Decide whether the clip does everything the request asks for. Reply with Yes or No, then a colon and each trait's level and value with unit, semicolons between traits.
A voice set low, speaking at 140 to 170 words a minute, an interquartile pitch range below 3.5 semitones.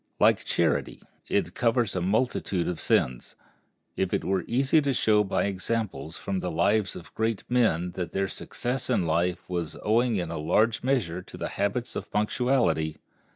No: low, 100 Hz; average, 165 wpm; average, 5.0 semitones